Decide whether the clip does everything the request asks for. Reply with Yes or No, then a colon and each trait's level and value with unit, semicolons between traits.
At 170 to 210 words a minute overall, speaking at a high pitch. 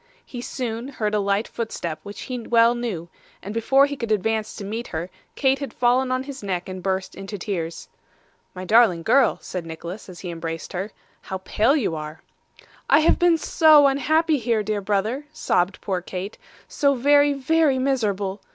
Yes: average, 180 wpm; high, 220 Hz